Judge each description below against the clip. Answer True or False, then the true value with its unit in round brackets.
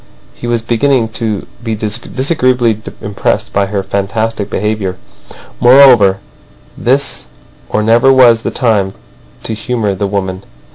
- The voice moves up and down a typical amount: True (3.2 semitones)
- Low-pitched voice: True (110 Hz)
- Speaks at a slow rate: True (125 wpm)